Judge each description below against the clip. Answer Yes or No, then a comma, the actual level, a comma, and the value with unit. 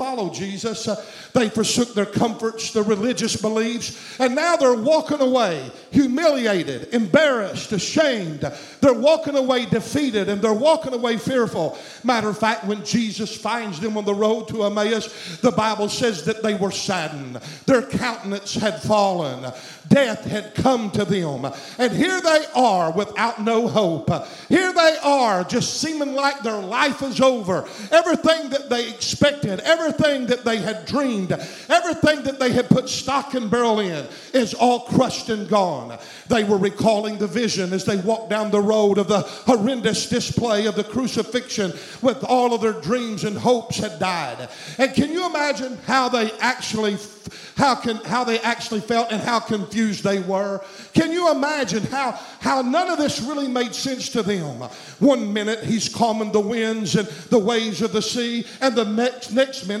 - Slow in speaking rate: No, average, 170 wpm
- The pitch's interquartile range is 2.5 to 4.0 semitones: Yes, average, 3.5 semitones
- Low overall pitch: No, high, 225 Hz